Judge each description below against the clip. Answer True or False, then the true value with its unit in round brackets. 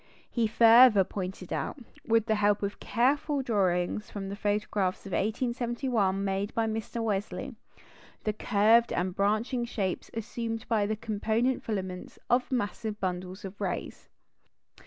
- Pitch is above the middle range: True (215 Hz)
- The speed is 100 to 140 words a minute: True (135 wpm)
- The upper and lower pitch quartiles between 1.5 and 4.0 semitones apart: True (2.9 semitones)